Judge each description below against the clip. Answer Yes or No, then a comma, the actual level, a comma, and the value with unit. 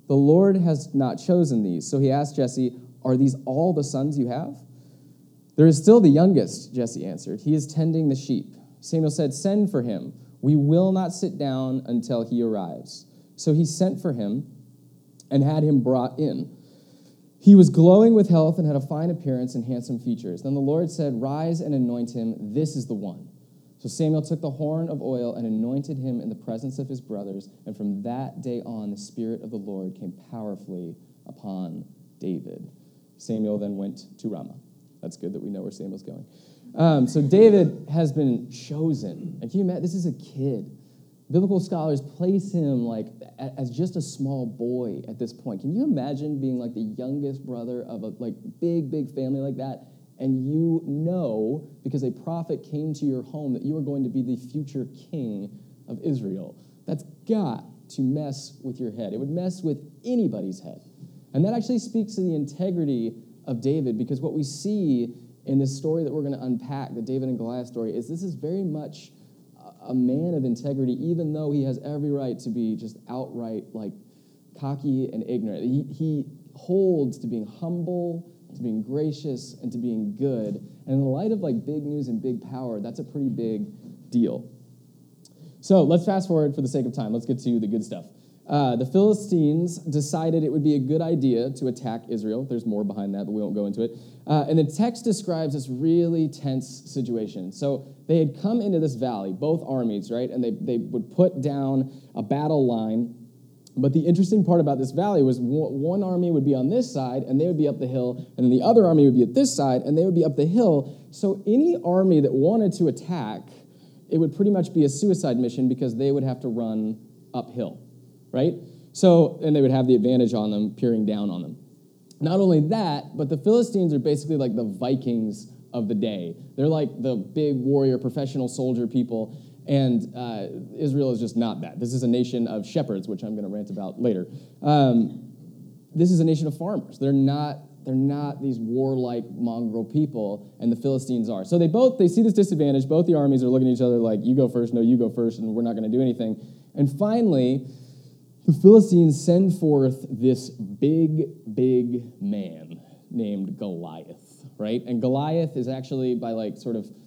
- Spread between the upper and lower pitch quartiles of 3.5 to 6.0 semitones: Yes, average, 4.5 semitones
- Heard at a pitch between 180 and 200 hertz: No, medium, 140 Hz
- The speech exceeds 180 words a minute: Yes, average, 200 wpm